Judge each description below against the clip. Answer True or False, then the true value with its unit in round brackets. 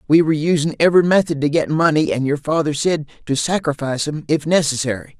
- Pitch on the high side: False (150 Hz)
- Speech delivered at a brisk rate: False (195 wpm)